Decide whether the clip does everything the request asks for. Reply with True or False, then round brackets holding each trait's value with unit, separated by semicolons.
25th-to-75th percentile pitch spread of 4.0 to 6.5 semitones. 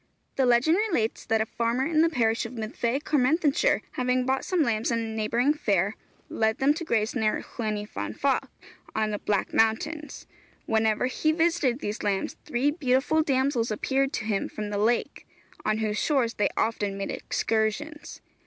True (4.7 semitones)